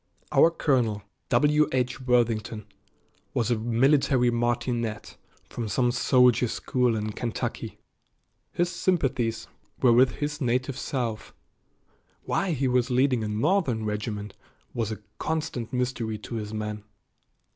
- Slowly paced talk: Yes, slow, 125 wpm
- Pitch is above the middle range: No, low, 120 Hz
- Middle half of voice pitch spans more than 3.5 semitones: No, average, 3.0 semitones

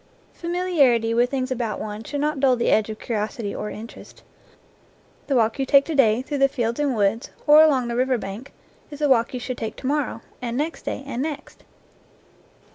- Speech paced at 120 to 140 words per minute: No, average, 200 wpm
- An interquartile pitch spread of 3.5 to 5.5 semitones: Yes, average, 3.8 semitones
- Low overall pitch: No, very high, 255 Hz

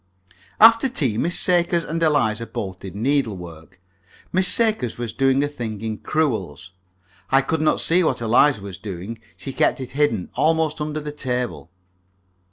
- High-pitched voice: No, low, 135 Hz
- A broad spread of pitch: Yes, wide, 6.5 semitones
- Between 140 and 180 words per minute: Yes, average, 160 wpm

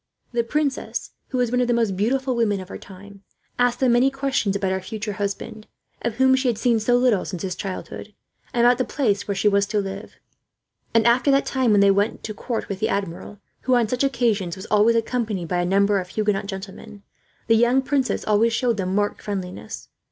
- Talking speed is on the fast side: Yes, fast, 220 wpm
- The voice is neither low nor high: No, high, 215 Hz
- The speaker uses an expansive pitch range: No, average, 3.6 semitones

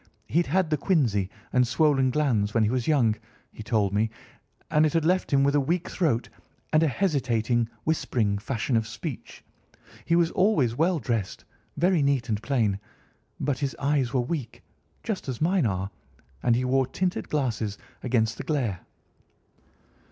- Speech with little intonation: No, wide, 5.4 semitones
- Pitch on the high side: No, low, 130 Hz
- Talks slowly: No, average, 165 wpm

